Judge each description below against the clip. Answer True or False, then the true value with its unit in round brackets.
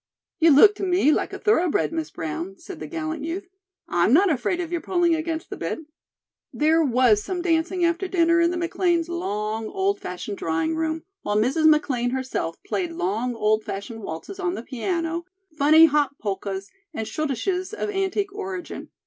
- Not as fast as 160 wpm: False (175 wpm)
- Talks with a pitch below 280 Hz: False (320 Hz)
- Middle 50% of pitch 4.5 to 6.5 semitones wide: False (7.1 semitones)